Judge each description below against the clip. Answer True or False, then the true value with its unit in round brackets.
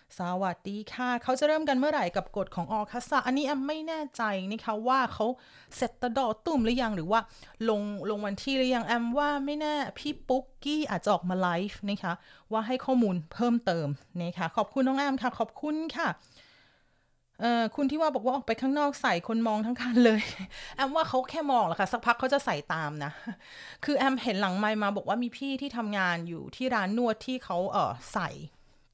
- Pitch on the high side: True (235 Hz)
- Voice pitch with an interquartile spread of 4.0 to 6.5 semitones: True (5.0 semitones)